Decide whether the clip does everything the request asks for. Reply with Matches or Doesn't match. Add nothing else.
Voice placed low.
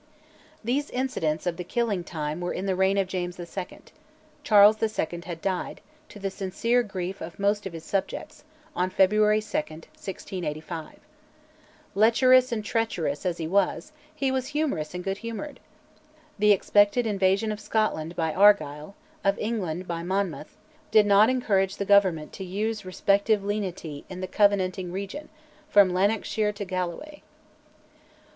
Doesn't match